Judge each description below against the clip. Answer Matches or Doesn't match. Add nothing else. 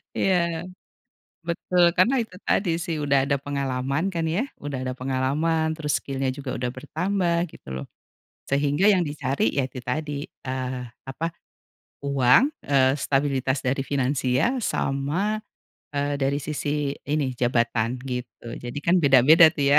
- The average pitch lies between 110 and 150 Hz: Matches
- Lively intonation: Doesn't match